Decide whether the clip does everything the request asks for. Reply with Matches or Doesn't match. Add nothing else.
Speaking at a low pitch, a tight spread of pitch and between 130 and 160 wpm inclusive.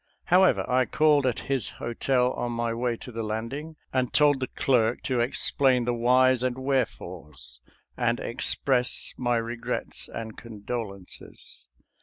Matches